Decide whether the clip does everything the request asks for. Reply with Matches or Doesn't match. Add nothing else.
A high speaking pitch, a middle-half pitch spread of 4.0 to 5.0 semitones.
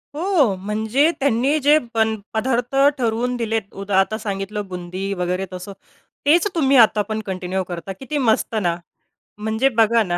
Matches